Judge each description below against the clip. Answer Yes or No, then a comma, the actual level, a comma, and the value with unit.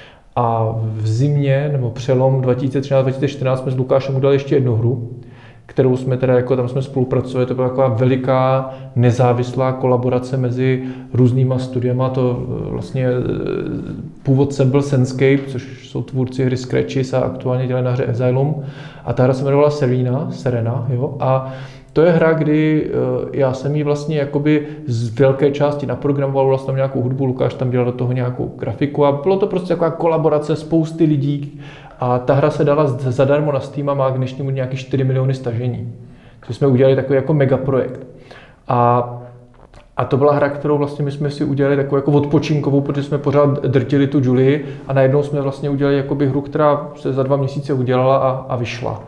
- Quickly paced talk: Yes, fast, 175 wpm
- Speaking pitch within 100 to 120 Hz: No, low, 135 Hz